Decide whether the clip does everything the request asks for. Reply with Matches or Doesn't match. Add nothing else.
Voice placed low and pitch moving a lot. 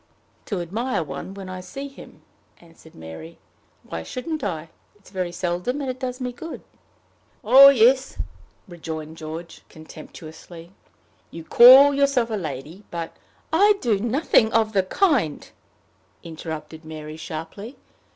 Doesn't match